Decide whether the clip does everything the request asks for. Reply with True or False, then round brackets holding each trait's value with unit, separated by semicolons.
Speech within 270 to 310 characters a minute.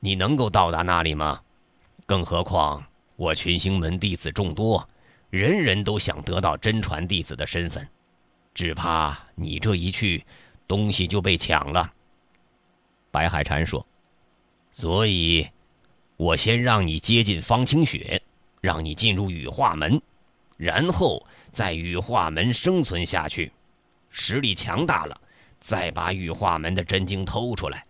False (200 characters per minute)